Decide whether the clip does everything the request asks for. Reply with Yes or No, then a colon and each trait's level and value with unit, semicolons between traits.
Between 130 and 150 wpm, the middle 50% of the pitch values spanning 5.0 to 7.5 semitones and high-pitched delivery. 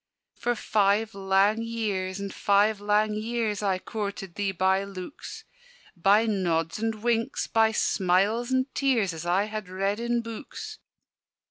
No: average, 140 wpm; average, 2.7 semitones; high, 210 Hz